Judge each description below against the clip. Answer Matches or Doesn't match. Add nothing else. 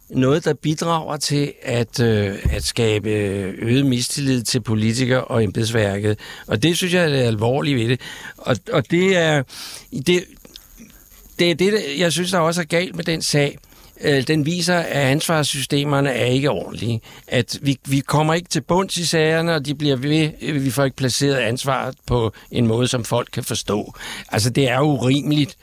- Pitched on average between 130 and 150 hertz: Matches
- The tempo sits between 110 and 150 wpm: Doesn't match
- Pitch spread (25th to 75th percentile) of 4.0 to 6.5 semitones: Matches